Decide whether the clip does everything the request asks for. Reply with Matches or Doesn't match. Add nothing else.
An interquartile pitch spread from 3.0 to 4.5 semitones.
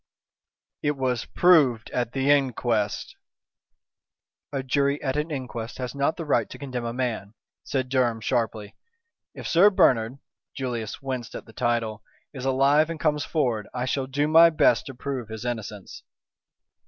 Matches